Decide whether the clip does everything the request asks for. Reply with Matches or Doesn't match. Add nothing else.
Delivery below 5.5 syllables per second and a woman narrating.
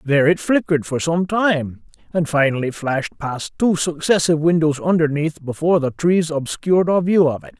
Doesn't match